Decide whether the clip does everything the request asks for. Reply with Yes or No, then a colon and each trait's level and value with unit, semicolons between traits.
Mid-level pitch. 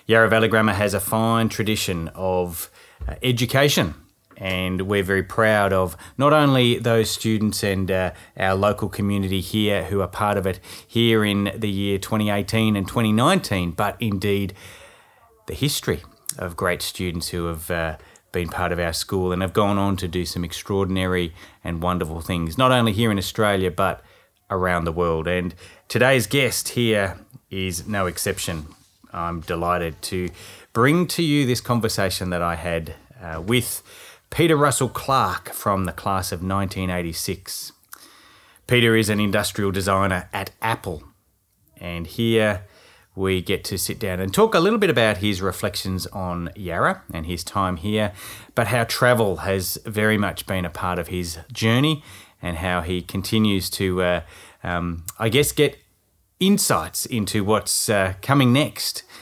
No: low, 100 Hz